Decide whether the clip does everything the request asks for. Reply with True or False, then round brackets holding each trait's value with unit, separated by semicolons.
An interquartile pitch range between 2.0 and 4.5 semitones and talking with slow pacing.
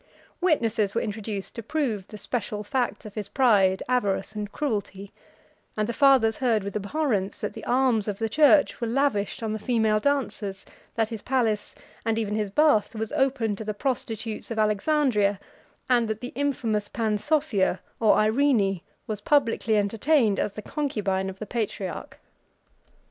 False (3.6 semitones; 160 wpm)